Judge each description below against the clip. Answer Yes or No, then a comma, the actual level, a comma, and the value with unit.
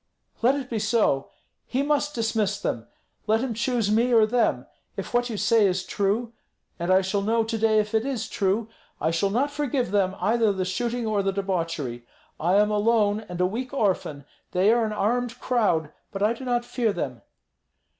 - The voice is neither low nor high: No, high, 215 Hz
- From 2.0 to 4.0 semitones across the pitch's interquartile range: Yes, average, 3.6 semitones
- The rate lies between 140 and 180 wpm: No, average, 195 wpm